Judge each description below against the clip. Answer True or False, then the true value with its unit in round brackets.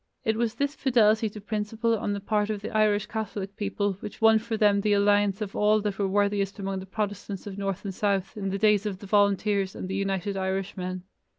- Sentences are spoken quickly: True (220 wpm)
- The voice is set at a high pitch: True (205 Hz)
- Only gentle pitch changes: True (1.5 semitones)